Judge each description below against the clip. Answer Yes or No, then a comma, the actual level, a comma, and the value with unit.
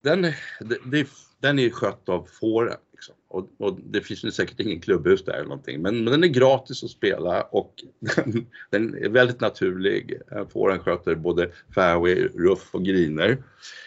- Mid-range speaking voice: Yes, medium, 145 Hz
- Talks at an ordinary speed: Yes, average, 165 wpm